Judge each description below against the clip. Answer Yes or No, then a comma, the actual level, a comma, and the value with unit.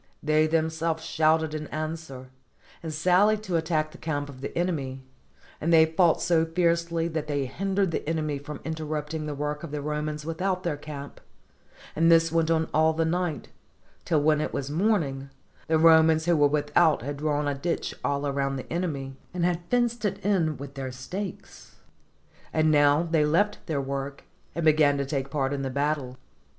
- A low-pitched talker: No, medium, 155 Hz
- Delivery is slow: No, average, 185 wpm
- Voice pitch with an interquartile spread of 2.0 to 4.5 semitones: Yes, narrow, 2.5 semitones